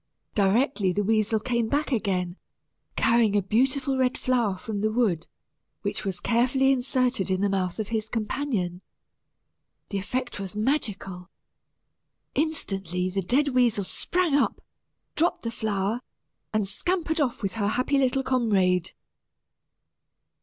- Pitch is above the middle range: Yes, high, 220 Hz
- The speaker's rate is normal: No, slow, 130 wpm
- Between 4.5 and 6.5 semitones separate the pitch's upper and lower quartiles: Yes, average, 4.8 semitones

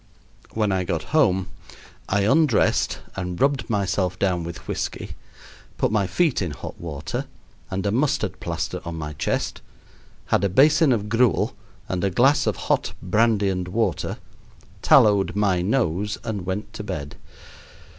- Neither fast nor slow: Yes, average, 150 wpm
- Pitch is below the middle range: Yes, low, 100 Hz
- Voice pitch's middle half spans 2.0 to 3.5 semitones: No, average, 3.9 semitones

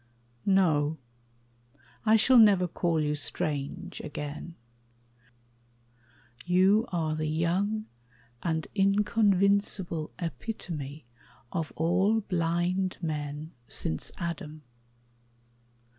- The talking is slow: Yes, slow, 80 wpm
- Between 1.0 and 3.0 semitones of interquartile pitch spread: No, average, 4.1 semitones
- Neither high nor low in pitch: Yes, medium, 170 Hz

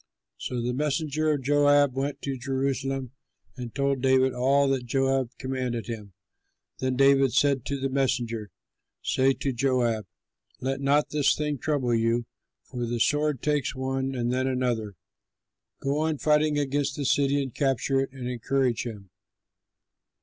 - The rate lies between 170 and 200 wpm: No, average, 155 wpm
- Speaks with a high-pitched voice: No, low, 135 Hz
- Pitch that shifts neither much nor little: No, narrow, 2.3 semitones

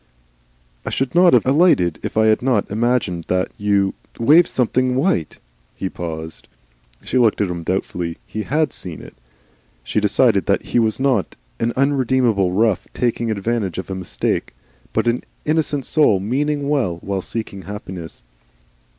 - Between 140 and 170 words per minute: Yes, average, 160 wpm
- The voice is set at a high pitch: No, low, 110 Hz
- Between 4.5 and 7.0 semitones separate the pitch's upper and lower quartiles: Yes, wide, 5.6 semitones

